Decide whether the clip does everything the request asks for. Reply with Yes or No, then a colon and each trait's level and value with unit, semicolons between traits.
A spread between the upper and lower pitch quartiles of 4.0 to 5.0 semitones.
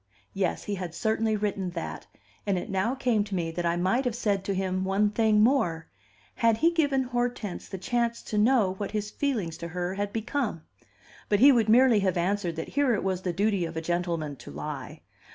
Yes: average, 4.4 semitones